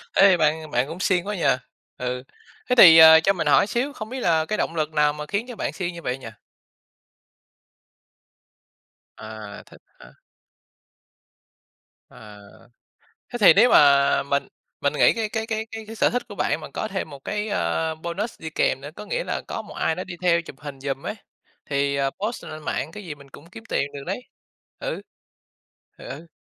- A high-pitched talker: No, medium, 160 Hz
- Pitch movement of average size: No, wide, 6.7 semitones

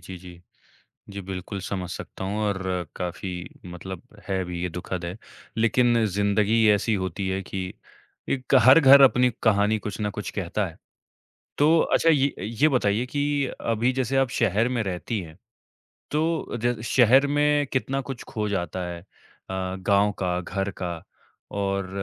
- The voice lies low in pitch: Yes, low, 105 Hz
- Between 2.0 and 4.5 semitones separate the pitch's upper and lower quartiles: No, average, 5.2 semitones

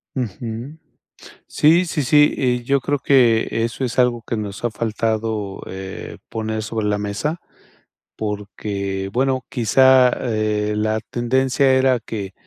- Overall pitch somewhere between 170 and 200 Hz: No, low, 115 Hz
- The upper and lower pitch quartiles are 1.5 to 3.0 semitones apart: No, average, 3.7 semitones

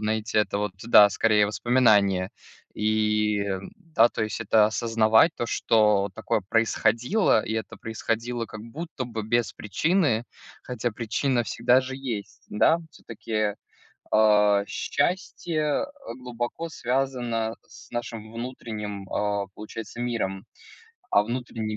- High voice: No, low, 115 Hz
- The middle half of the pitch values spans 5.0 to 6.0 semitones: No, narrow, 2.4 semitones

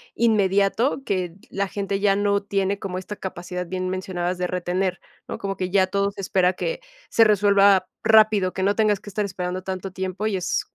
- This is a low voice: No, high, 195 Hz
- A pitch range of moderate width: No, narrow, 1.7 semitones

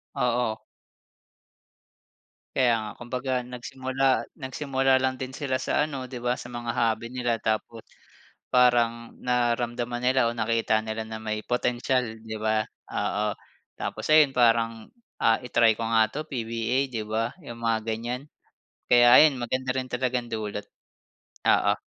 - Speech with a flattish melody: Yes, narrow, 2.2 semitones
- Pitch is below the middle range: Yes, low, 120 Hz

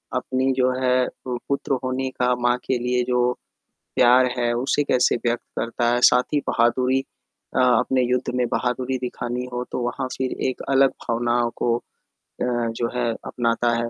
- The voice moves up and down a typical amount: No, narrow, 1.1 semitones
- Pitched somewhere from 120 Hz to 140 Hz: Yes, low, 125 Hz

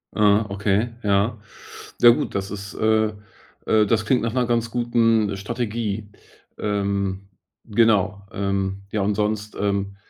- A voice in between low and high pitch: No, low, 105 Hz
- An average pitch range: No, narrow, 2.3 semitones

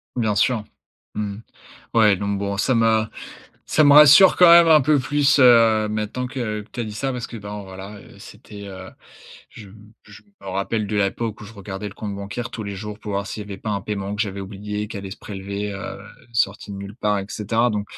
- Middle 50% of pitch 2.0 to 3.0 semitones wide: Yes, narrow, 2.4 semitones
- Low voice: Yes, low, 105 Hz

